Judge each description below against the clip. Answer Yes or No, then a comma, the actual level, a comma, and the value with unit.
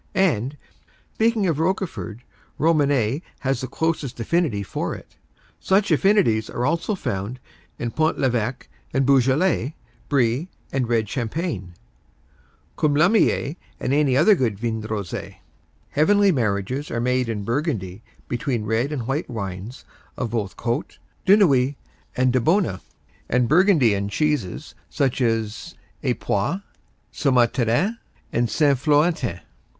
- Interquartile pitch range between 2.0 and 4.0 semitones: No, wide, 5.6 semitones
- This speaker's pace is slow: Yes, slow, 120 wpm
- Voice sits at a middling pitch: No, low, 130 Hz